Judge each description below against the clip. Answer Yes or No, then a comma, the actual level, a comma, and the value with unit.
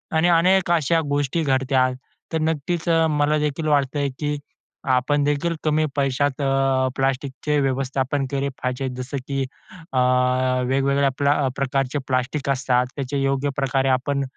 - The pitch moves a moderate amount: No, narrow, 1.8 semitones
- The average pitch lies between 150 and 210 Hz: No, medium, 140 Hz